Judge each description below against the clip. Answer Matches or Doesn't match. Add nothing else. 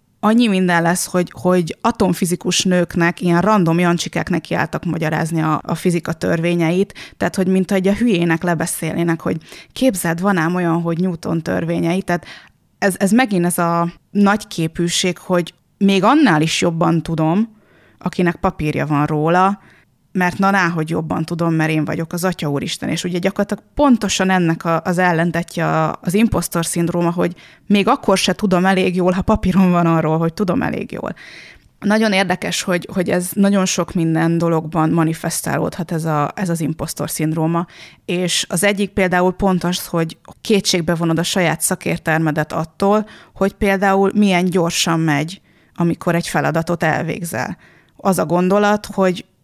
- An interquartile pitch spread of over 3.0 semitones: Doesn't match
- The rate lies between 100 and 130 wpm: Doesn't match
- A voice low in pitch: Doesn't match